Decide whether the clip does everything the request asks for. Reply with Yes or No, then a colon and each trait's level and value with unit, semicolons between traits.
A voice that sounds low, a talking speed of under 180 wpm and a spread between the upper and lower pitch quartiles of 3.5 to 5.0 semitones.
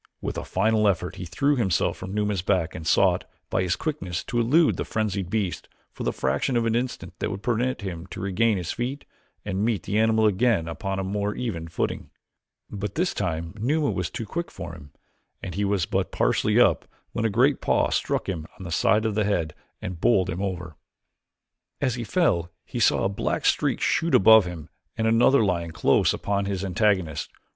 No: low, 100 Hz; average, 200 wpm; average, 4.1 semitones